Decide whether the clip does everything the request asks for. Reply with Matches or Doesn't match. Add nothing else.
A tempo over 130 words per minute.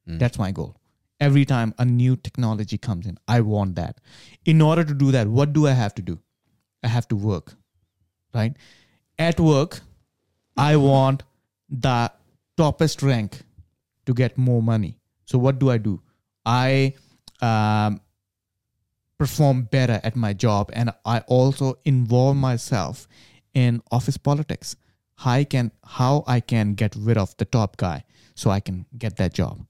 Matches